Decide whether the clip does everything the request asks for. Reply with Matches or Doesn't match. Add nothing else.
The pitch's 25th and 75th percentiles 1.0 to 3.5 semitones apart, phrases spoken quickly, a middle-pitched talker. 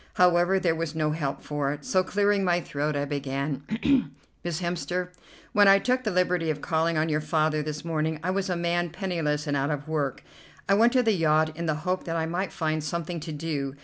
Matches